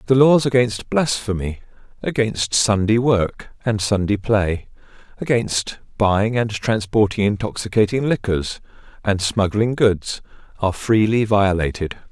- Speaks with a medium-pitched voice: No, low, 110 Hz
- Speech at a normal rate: No, slow, 110 wpm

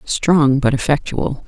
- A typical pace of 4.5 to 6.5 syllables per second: No, 3.7 syllables/s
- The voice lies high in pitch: No, medium, 140 Hz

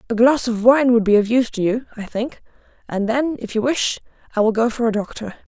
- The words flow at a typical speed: No, fast, 250 wpm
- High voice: Yes, high, 230 Hz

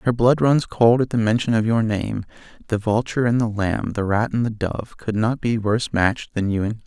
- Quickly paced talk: Yes, fast, 255 wpm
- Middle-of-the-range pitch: No, low, 110 Hz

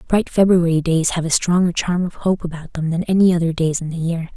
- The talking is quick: Yes, fast, 250 wpm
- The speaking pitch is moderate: Yes, medium, 170 Hz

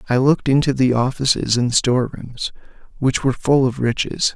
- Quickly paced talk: No, average, 180 wpm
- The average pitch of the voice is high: No, low, 130 Hz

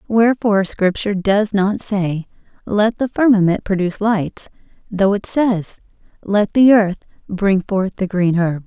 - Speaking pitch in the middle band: No, high, 200 Hz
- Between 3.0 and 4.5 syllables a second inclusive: Yes, 4.3 syllables/s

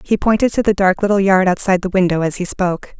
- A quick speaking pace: Yes, fast, 260 wpm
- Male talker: No, female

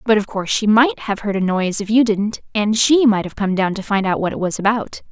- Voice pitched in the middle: No, high, 210 Hz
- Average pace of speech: No, fast, 295 wpm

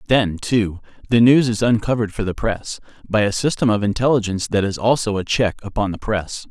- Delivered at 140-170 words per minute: No, fast, 205 wpm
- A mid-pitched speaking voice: No, low, 110 Hz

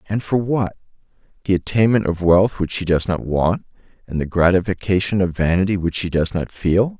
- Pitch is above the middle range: No, very low, 95 Hz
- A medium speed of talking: Yes, average, 180 wpm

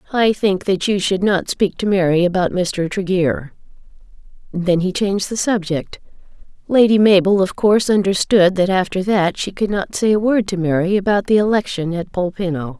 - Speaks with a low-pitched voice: No, high, 190 Hz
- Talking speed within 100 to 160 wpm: No, average, 180 wpm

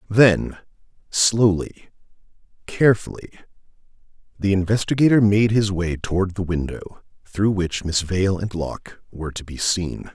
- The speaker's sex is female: No, male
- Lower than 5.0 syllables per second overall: Yes, 4.6 syllables/s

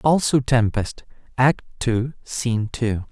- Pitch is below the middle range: Yes, low, 120 Hz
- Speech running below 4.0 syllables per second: Yes, 3.7 syllables/s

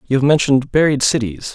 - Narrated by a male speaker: Yes, male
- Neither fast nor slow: Yes, average, 195 wpm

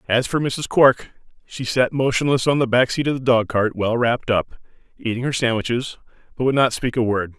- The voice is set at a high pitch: No, low, 125 Hz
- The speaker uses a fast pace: Yes, fast, 210 wpm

